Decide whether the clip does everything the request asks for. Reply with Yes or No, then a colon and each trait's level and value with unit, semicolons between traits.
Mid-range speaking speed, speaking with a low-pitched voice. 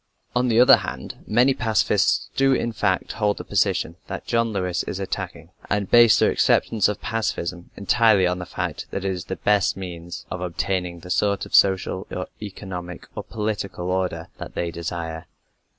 Yes: average, 180 wpm; very low, 95 Hz